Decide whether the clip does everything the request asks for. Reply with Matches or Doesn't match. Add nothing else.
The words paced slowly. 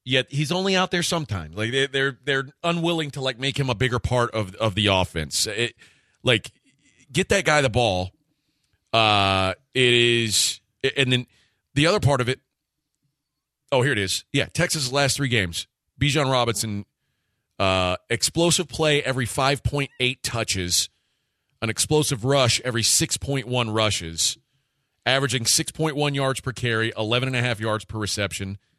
Doesn't match